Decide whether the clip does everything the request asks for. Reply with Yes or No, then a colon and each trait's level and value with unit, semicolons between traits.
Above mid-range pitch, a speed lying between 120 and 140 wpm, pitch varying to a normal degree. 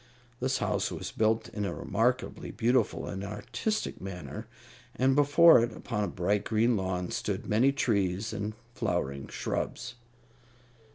No: low, 110 Hz; slow, 135 wpm; average, 4.2 semitones